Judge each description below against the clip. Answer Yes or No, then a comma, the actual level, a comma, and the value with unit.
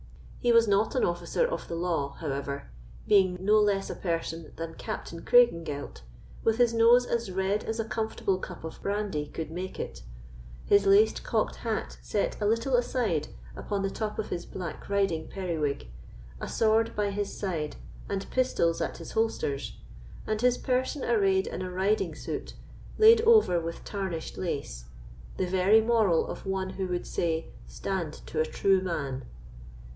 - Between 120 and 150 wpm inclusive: No, average, 165 wpm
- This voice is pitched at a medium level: No, high, 195 Hz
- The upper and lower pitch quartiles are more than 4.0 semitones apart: Yes, average, 4.8 semitones